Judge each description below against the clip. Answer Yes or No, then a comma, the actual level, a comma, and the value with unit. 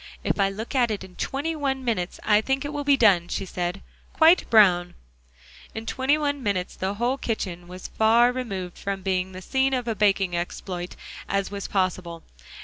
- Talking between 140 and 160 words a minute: No, average, 195 wpm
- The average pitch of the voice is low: No, high, 205 Hz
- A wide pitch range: Yes, wide, 5.8 semitones